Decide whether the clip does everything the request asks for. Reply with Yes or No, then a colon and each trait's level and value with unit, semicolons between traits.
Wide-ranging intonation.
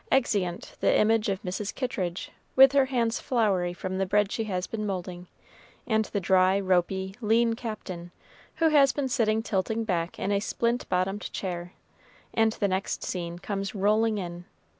No: average, 3.5 semitones